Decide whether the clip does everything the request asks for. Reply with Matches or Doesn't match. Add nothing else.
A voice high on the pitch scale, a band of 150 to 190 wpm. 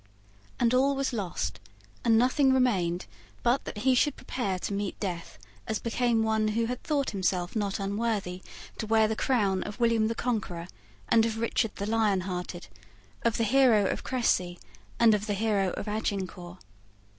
Matches